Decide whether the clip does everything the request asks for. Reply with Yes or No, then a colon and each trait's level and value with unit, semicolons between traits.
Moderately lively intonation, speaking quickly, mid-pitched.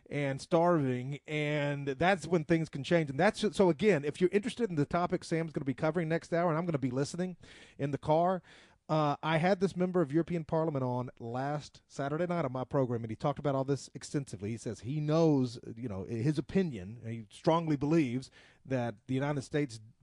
Yes: average, 4.3 semitones; fast, 215 wpm; medium, 150 Hz